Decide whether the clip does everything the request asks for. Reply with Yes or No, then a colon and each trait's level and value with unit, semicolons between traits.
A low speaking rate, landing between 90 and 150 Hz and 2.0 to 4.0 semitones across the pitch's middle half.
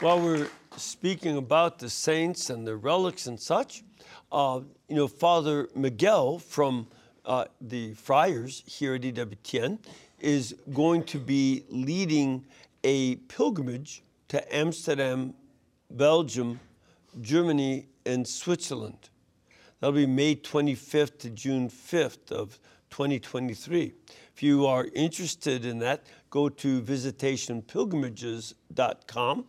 Yes: slow, 110 wpm; low, 135 Hz; average, 3.6 semitones